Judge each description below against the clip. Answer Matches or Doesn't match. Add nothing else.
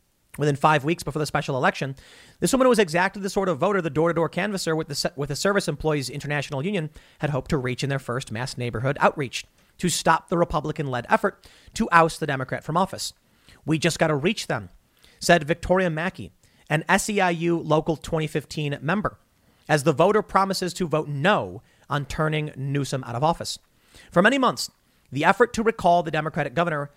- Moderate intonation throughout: Matches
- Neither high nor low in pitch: Matches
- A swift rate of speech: Doesn't match